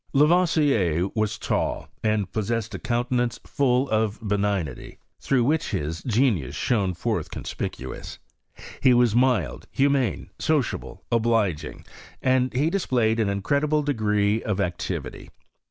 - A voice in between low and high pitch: No, low, 115 Hz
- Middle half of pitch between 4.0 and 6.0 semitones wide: Yes, average, 4.4 semitones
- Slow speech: Yes, slow, 120 wpm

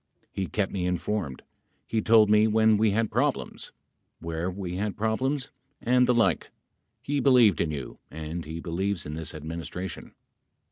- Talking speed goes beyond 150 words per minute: Yes, average, 160 wpm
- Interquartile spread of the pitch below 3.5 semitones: No, average, 4.9 semitones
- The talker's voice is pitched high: No, low, 100 Hz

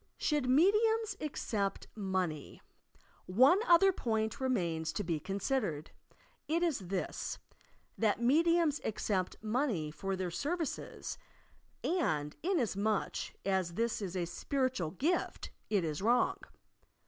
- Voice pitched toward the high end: Yes, high, 220 Hz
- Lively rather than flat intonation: Yes, wide, 8.4 semitones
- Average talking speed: No, slow, 120 wpm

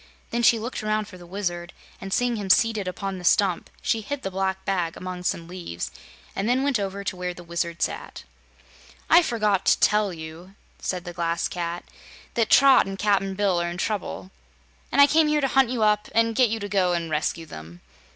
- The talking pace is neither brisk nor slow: No, fast, 210 wpm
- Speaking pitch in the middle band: No, high, 195 Hz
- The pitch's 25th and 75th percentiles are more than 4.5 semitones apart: No, average, 4.0 semitones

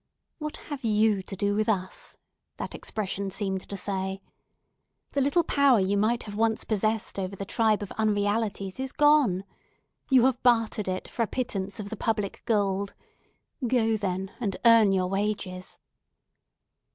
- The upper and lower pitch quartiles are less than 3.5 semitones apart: Yes, average, 2.8 semitones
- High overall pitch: Yes, high, 210 Hz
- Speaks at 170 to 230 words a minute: No, average, 155 wpm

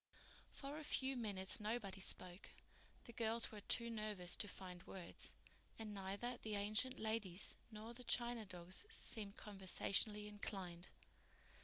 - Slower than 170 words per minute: Yes, slow, 135 wpm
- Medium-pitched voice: No, high, 210 Hz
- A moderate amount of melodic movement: Yes, average, 3.2 semitones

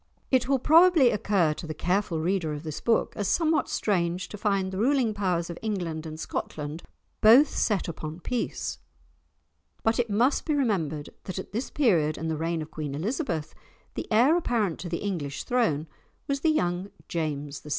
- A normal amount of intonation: No, wide, 6.7 semitones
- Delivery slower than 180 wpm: No, average, 185 wpm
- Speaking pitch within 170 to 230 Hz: Yes, high, 190 Hz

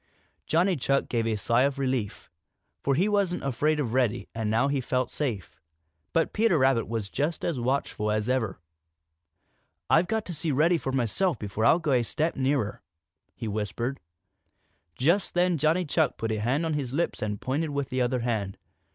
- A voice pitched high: No, low, 135 Hz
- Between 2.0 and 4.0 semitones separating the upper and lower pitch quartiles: No, wide, 5.4 semitones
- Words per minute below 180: No, average, 185 wpm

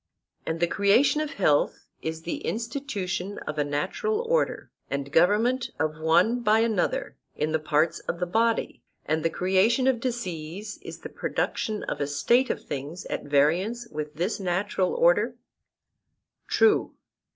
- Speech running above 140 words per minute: Yes, average, 150 wpm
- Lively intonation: Yes, wide, 6.9 semitones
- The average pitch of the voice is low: No, high, 190 Hz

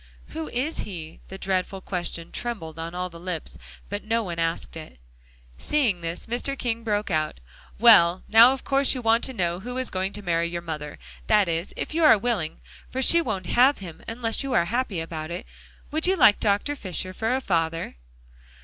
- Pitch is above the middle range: Yes, high, 195 Hz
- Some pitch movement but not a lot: No, wide, 6.0 semitones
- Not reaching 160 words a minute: No, fast, 205 wpm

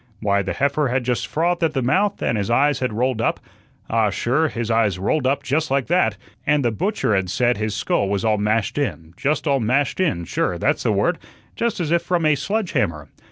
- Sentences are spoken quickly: Yes, fast, 225 wpm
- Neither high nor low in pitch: No, low, 130 Hz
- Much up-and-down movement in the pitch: Yes, wide, 6.1 semitones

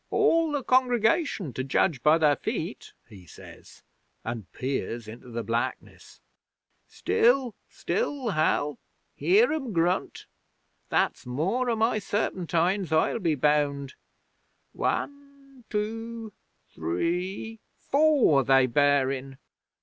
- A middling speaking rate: No, slow, 110 wpm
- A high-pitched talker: No, medium, 175 Hz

